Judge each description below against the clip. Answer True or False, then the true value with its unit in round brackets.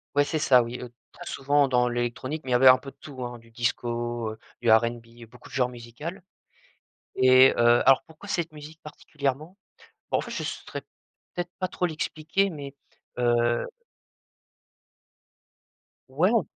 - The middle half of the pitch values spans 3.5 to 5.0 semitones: True (4.1 semitones)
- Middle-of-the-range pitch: False (130 Hz)